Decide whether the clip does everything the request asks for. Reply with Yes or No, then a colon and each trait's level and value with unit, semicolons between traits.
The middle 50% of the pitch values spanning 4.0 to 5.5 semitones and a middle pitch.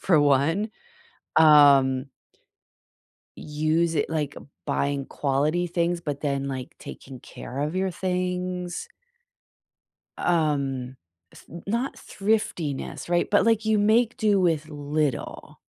Yes: average, 4.3 semitones; medium, 155 Hz